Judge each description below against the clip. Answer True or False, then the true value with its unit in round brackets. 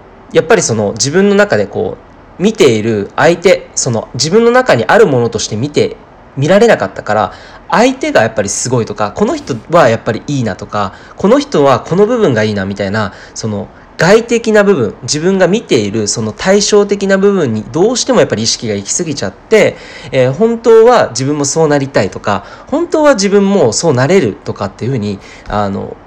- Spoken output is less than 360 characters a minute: False (380 characters per minute)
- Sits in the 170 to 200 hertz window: False (145 Hz)